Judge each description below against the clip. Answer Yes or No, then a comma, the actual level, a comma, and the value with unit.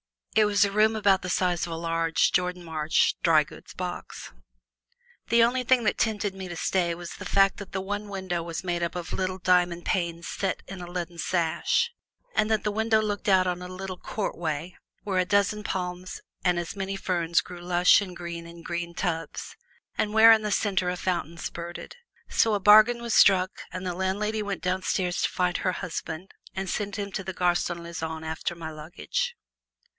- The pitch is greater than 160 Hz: Yes, medium, 185 Hz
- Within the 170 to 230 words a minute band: Yes, average, 200 wpm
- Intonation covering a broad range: No, average, 2.8 semitones